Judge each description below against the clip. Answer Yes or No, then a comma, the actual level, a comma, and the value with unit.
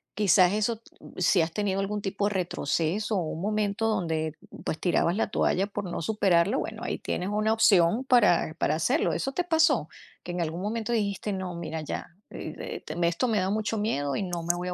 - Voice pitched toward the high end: Yes, high, 195 Hz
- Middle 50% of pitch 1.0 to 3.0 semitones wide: No, average, 3.9 semitones